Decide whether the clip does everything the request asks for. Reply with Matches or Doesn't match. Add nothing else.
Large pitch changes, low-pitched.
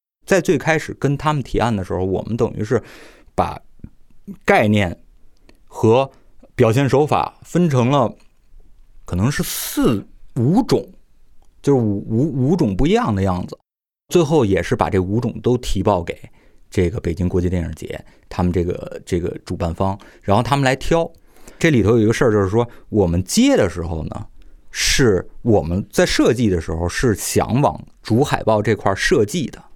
Matches